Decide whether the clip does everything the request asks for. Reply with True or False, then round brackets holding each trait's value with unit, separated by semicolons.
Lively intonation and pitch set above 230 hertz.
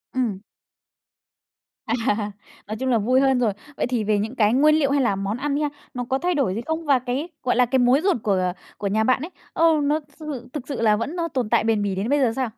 False (4.7 semitones; 250 Hz)